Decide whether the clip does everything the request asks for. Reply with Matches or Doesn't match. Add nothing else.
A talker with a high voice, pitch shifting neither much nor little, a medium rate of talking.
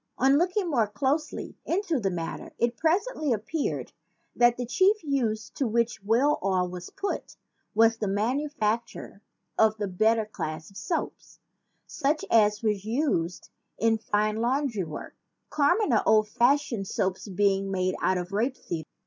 Doesn't match